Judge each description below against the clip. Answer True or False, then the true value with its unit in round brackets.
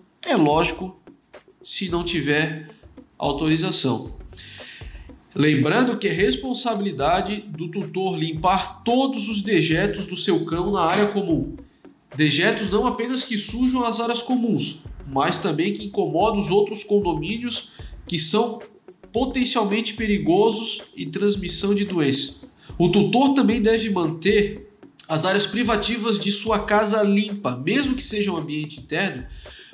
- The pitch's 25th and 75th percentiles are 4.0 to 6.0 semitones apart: True (4.6 semitones)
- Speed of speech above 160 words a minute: False (125 wpm)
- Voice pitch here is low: False (205 Hz)